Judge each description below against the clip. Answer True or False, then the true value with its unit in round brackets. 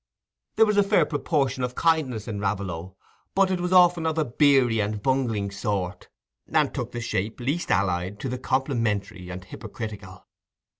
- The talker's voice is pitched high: False (120 Hz)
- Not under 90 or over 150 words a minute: False (165 wpm)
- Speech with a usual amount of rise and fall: False (6.6 semitones)